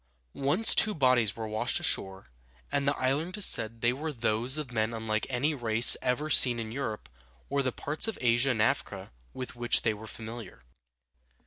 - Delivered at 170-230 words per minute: Yes, average, 180 wpm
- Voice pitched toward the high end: No, low, 120 Hz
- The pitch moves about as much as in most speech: Yes, average, 4.0 semitones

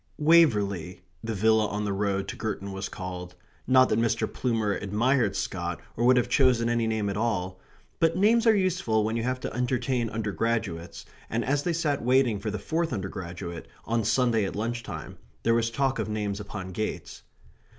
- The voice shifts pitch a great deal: No, average, 3.9 semitones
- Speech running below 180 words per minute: No, average, 185 wpm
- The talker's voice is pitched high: No, low, 115 Hz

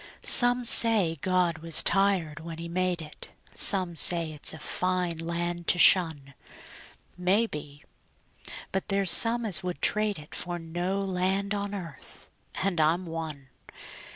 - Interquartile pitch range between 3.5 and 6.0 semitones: No, average, 3.1 semitones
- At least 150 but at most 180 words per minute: No, average, 140 wpm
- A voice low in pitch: No, medium, 175 Hz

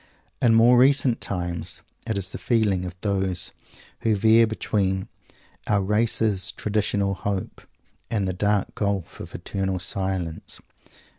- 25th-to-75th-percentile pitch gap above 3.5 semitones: No, narrow, 2.6 semitones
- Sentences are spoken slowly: Yes, slow, 130 wpm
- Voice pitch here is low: Yes, low, 100 Hz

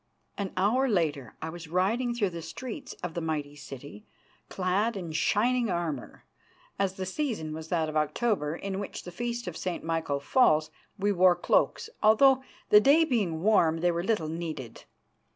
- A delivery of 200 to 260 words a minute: No, average, 170 wpm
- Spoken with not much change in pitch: No, average, 5.2 semitones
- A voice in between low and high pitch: Yes, medium, 180 Hz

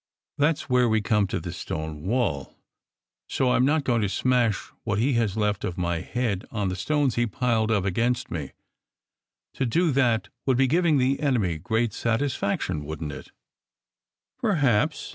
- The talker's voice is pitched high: No, low, 115 Hz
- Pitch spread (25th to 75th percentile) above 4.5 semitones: Yes, average, 5.1 semitones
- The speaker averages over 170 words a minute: Yes, average, 180 wpm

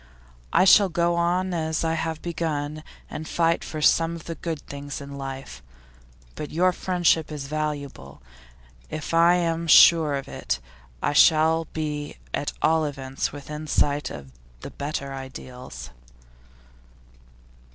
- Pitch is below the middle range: No, medium, 155 Hz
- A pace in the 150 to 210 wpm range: No, average, 140 wpm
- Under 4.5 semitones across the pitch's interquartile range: Yes, average, 2.8 semitones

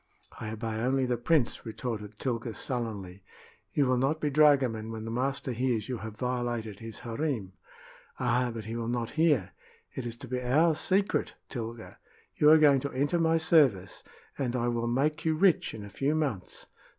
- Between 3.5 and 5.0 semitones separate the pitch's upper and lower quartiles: Yes, average, 4.1 semitones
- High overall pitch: No, low, 125 Hz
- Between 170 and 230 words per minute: Yes, average, 185 wpm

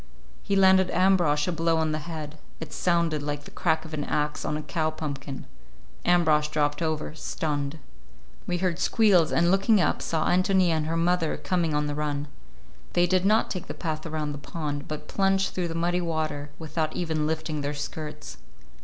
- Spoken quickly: No, average, 185 wpm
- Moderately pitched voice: Yes, medium, 160 Hz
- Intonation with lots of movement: No, average, 2.7 semitones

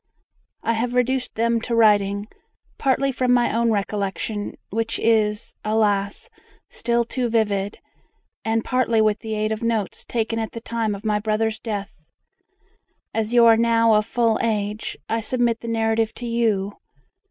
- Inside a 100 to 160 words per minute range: Yes, average, 155 wpm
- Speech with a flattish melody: Yes, narrow, 1.7 semitones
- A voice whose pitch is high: Yes, high, 225 Hz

